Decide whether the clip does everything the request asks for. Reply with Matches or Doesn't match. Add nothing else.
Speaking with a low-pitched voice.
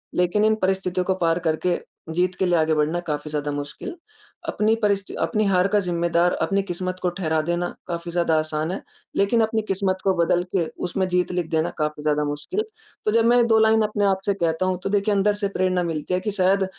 Doesn't match